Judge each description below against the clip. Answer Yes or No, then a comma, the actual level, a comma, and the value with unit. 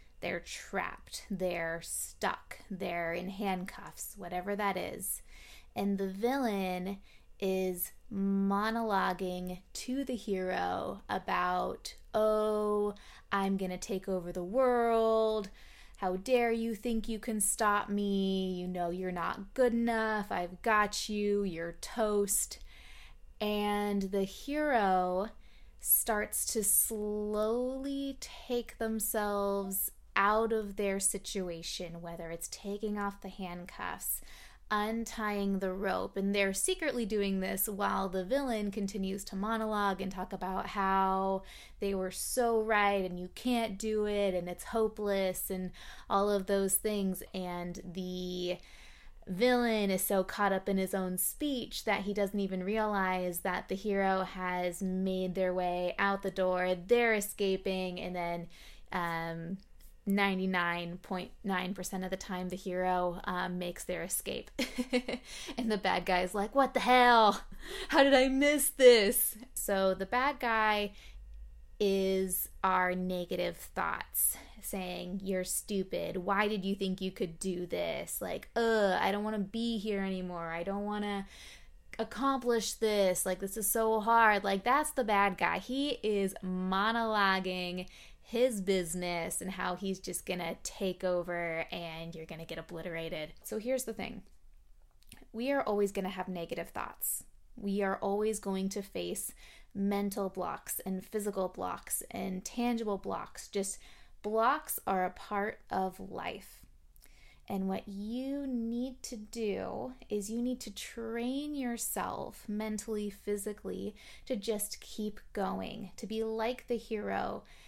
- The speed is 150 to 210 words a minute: No, average, 140 wpm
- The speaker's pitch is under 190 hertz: No, high, 200 Hz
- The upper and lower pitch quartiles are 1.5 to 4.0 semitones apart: Yes, average, 2.9 semitones